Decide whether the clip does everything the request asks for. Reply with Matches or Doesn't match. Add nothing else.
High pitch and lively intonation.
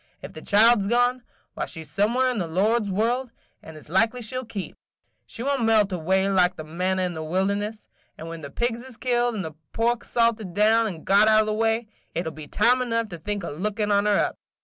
Doesn't match